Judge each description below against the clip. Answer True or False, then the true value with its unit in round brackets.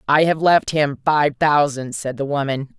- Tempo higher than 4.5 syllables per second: False (4.2 syllables/s)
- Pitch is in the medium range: True (145 Hz)